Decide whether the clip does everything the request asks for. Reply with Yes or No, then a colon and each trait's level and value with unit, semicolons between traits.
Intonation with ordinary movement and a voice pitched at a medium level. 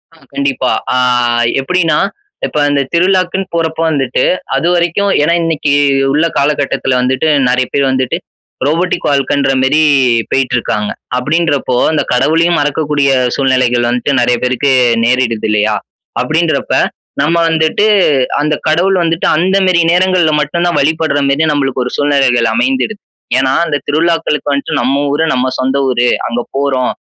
Yes: average, 4.1 semitones; medium, 145 Hz